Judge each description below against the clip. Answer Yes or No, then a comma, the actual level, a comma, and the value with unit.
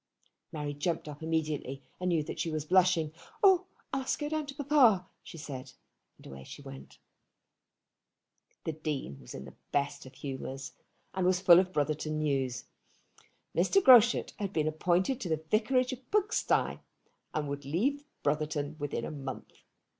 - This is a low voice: No, medium, 155 Hz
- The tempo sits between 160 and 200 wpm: Yes, average, 165 wpm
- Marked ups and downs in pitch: Yes, wide, 6.4 semitones